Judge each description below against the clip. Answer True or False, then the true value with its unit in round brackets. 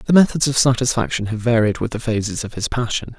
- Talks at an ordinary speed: False (225 wpm)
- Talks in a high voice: False (120 Hz)